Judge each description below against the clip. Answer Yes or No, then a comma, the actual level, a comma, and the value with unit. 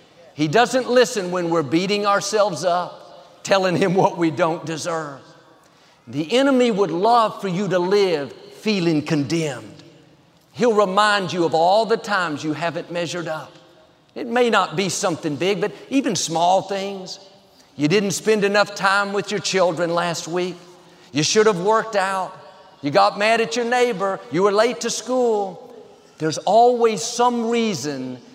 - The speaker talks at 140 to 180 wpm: Yes, average, 160 wpm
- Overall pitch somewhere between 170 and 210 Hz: Yes, high, 190 Hz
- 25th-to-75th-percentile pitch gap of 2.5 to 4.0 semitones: No, average, 4.5 semitones